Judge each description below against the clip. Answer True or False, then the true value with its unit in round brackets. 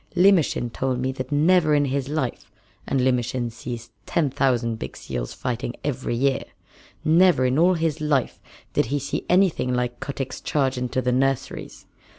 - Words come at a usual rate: True (165 wpm)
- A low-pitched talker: True (130 Hz)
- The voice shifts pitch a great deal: False (3.3 semitones)